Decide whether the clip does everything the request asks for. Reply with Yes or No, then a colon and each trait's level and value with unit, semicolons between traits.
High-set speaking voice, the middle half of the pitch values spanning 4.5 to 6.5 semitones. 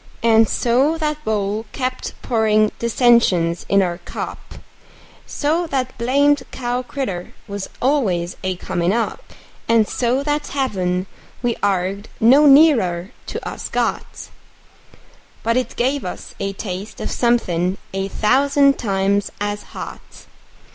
Yes: high, 225 Hz; wide, 5.4 semitones